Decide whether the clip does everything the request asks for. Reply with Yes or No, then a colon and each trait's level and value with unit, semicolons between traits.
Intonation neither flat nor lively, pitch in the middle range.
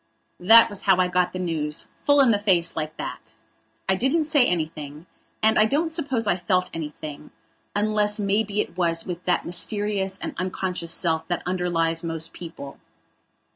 Yes: average, 4.1 semitones; medium, 180 Hz